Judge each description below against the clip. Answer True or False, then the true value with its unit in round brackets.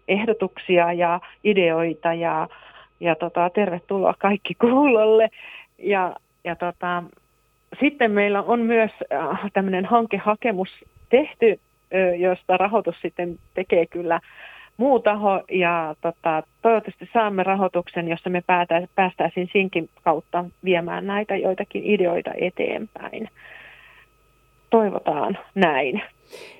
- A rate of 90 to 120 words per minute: True (100 wpm)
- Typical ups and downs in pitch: True (3.3 semitones)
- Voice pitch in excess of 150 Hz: True (185 Hz)